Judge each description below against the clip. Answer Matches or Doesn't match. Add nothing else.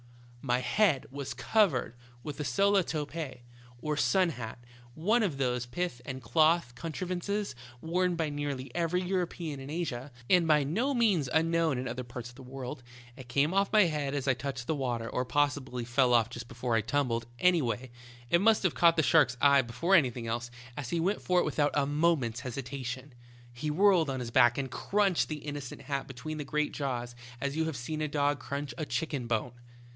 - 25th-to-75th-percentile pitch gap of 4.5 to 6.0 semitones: Matches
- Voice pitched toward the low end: Doesn't match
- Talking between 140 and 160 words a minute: Doesn't match